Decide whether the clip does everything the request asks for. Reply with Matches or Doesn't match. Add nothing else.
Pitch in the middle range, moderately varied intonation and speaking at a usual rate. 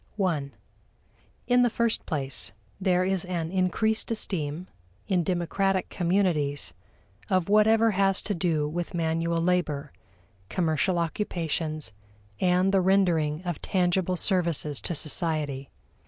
Doesn't match